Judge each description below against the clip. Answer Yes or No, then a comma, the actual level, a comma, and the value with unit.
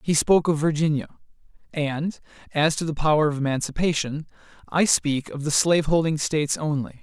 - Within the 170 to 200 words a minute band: No, average, 160 wpm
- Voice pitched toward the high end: No, medium, 150 Hz